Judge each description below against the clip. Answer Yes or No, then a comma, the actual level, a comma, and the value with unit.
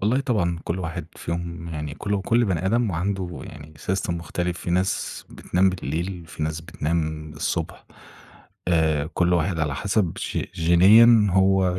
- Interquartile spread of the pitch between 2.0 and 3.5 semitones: Yes, average, 3.0 semitones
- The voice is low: Yes, very low, 85 Hz